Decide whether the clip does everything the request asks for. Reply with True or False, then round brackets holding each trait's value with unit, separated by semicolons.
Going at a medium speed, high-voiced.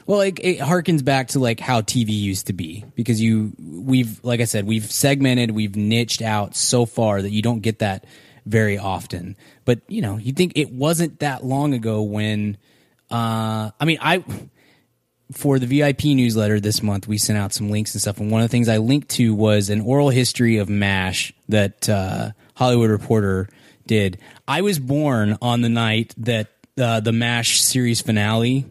False (190 wpm; 115 Hz)